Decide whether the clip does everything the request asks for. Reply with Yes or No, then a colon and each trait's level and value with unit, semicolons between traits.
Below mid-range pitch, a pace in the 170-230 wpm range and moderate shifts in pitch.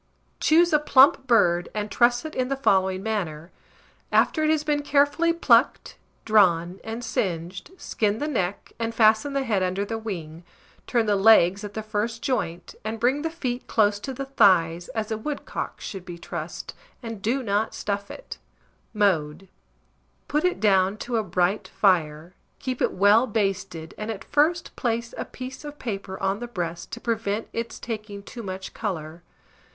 No: high, 215 Hz; average, 175 wpm; average, 4.5 semitones